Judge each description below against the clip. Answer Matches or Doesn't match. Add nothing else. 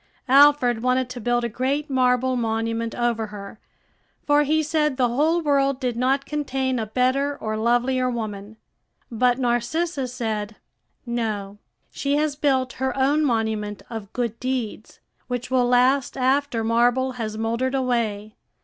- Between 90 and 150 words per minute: Matches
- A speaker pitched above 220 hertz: Matches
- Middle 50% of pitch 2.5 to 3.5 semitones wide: Matches